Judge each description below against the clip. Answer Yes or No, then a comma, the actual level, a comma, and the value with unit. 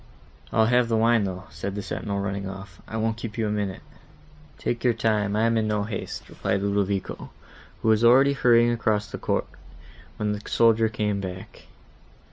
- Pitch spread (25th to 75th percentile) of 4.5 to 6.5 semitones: No, narrow, 2.4 semitones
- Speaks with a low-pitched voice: Yes, low, 105 Hz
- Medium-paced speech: Yes, average, 185 wpm